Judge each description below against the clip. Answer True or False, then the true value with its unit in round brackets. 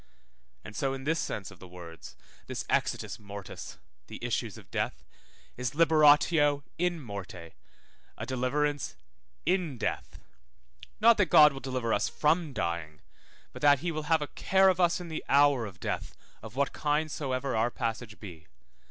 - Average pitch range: False (6.1 semitones)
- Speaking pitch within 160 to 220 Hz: False (140 Hz)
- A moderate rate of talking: True (165 wpm)